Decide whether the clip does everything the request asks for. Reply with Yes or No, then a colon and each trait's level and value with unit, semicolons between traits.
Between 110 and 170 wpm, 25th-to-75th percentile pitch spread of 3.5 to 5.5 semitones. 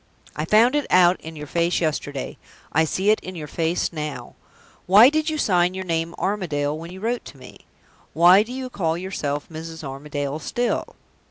No: average, 185 wpm; average, 4.3 semitones